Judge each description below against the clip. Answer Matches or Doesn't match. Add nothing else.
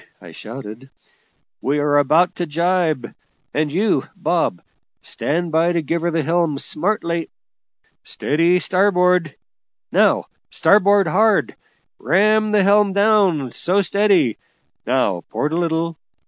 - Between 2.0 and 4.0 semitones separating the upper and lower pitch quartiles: Doesn't match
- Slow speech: Matches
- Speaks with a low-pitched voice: Doesn't match